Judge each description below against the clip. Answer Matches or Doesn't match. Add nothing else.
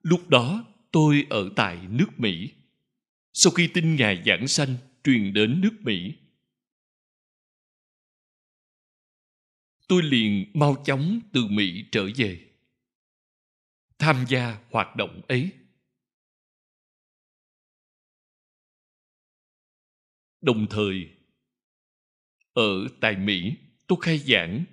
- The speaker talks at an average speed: Doesn't match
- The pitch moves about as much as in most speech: Doesn't match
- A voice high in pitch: Doesn't match